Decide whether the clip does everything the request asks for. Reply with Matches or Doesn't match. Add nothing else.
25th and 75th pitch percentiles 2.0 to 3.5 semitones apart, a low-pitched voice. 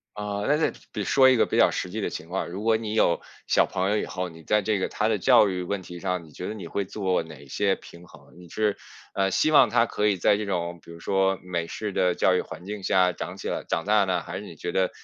Matches